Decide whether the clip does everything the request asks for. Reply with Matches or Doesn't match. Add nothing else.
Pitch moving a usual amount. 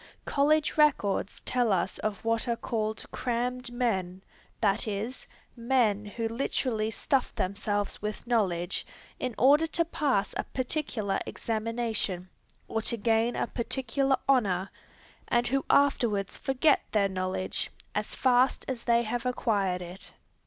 Matches